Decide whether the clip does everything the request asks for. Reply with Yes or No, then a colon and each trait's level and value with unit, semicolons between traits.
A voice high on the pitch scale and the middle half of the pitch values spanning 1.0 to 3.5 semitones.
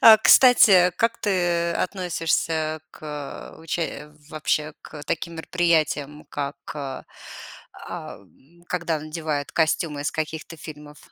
No: medium, 160 Hz; narrow, 2.5 semitones